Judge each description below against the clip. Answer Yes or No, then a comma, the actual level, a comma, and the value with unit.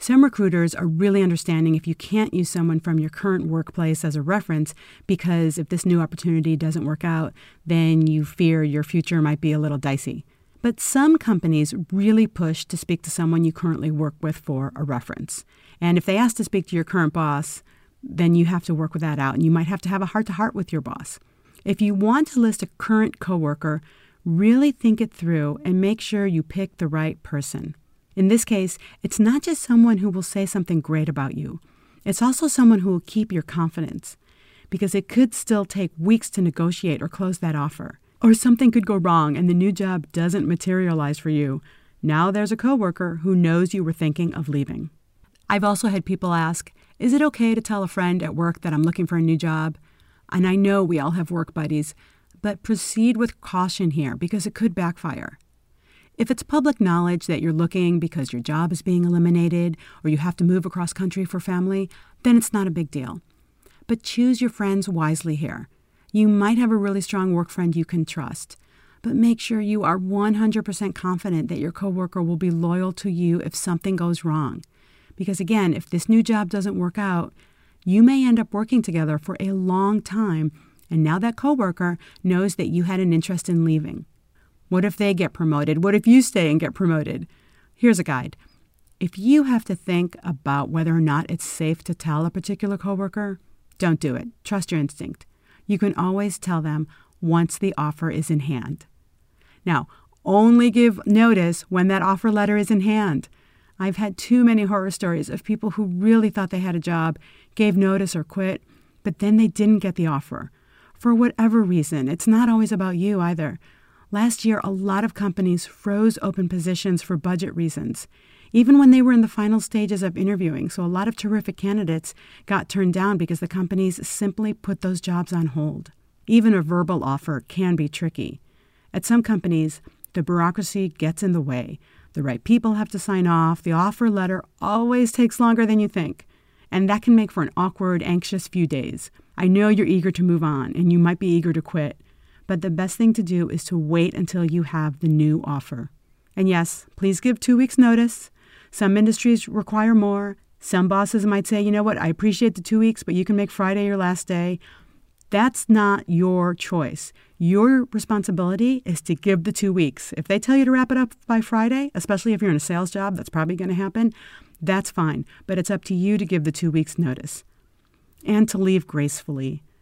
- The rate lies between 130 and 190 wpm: No, fast, 205 wpm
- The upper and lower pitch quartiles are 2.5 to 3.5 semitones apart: No, average, 4.1 semitones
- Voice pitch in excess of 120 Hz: Yes, medium, 185 Hz